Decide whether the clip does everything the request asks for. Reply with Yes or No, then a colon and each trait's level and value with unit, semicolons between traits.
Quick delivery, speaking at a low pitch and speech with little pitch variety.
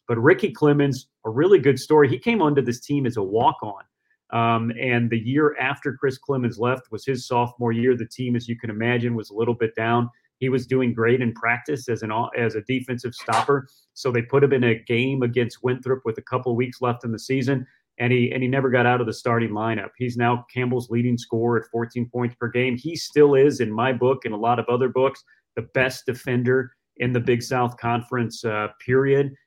Yes: fast, 225 wpm; low, 125 Hz; narrow, 1.9 semitones